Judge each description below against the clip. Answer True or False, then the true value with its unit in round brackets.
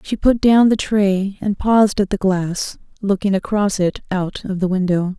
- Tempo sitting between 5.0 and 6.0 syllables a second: False (4.4 syllables/s)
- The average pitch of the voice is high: True (195 Hz)